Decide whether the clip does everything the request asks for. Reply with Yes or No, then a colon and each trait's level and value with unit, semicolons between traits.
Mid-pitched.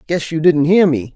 Yes: medium, 155 Hz